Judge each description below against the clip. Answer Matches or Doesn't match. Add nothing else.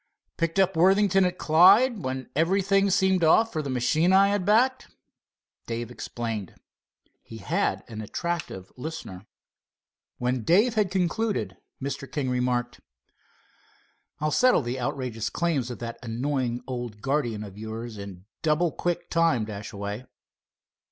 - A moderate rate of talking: Doesn't match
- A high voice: Doesn't match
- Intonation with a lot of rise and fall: Matches